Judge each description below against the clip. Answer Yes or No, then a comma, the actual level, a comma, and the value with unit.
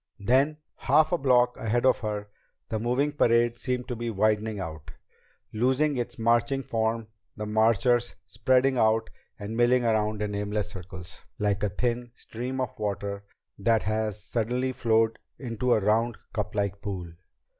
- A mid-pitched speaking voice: No, low, 115 Hz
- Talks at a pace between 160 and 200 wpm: No, average, 150 wpm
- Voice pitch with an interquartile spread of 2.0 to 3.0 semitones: Yes, average, 2.7 semitones